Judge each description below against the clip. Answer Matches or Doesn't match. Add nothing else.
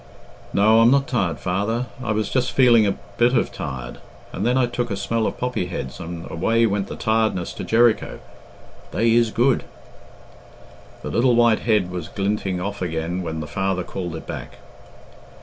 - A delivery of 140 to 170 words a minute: Doesn't match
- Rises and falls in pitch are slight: Doesn't match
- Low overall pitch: Matches